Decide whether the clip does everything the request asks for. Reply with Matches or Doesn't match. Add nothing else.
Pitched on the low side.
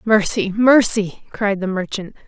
Doesn't match